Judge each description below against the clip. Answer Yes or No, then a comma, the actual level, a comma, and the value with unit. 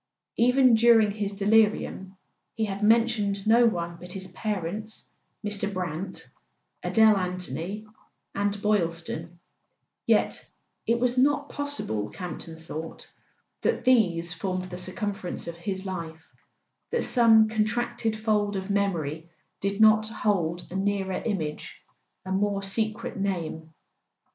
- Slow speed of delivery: Yes, slow, 130 wpm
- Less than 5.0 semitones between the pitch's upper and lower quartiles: Yes, average, 3.6 semitones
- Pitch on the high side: Yes, high, 200 Hz